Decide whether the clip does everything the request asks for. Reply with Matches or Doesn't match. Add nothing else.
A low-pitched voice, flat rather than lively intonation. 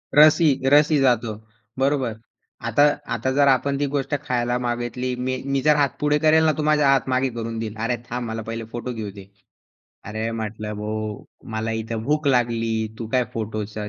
Doesn't match